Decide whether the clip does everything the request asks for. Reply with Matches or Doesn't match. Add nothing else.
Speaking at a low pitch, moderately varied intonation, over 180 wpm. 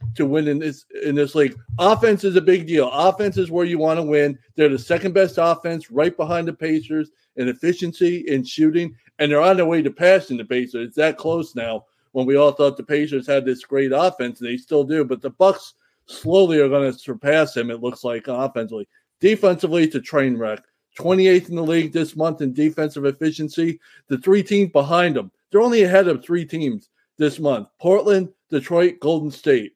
Doesn't match